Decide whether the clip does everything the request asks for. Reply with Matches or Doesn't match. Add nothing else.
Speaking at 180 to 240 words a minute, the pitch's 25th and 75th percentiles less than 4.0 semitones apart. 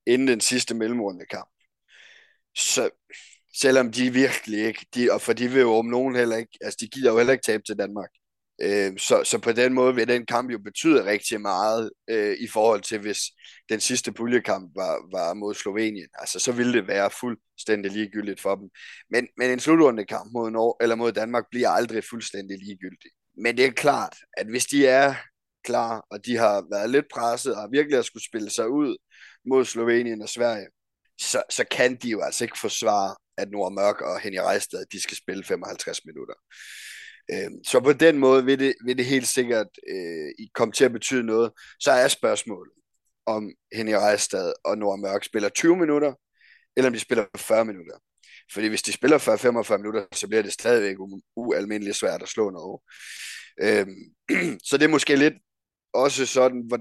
Doesn't match